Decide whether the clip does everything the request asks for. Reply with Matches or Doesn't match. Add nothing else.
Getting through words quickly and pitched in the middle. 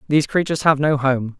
Matches